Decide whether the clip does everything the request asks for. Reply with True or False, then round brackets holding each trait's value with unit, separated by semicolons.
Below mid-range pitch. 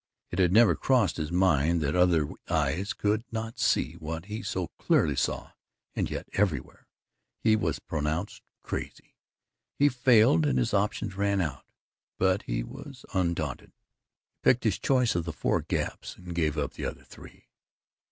True (90 Hz)